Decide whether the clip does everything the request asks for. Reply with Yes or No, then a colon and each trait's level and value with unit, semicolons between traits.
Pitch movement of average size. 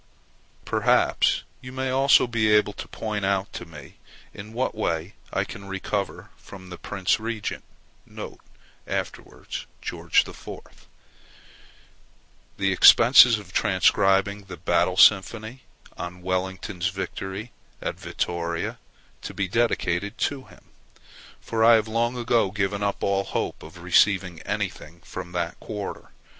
Yes: average, 3.1 semitones